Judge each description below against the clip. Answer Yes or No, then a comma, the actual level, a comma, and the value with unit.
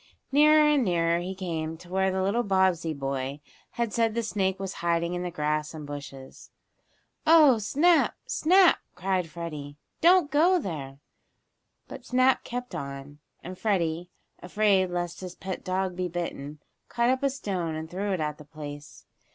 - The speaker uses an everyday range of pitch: No, wide, 6.1 semitones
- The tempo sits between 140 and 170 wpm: Yes, average, 165 wpm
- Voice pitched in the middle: Yes, medium, 180 Hz